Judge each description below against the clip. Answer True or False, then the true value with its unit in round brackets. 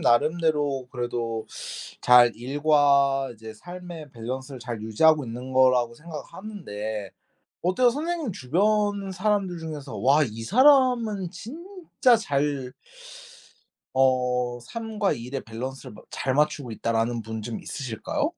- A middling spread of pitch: False (7.8 semitones)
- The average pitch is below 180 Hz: True (140 Hz)